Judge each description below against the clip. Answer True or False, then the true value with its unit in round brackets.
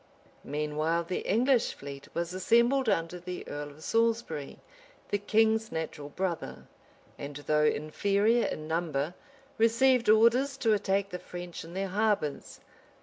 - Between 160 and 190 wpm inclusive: False (140 wpm)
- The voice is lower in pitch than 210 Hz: True (185 Hz)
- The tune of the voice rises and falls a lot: True (6.2 semitones)